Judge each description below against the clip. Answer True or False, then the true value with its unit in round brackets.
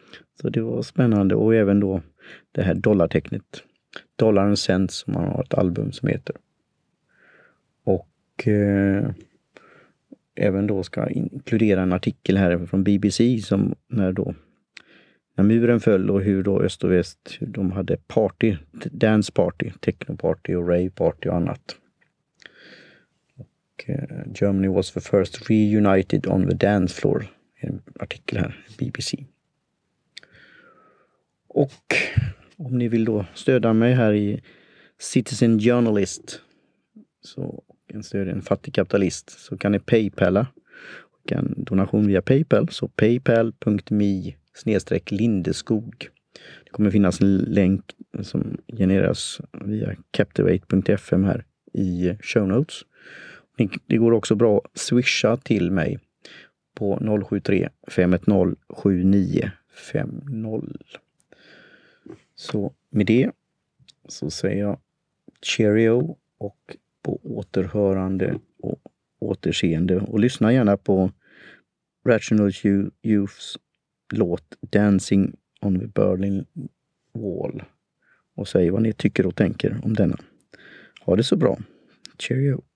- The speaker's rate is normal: False (120 wpm)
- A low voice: True (100 Hz)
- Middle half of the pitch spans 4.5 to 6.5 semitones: False (2.8 semitones)